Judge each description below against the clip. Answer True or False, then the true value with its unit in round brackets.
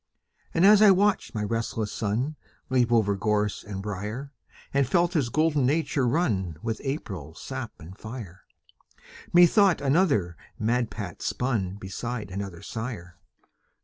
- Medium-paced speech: False (130 wpm)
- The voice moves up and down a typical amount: False (6.2 semitones)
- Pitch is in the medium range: False (115 Hz)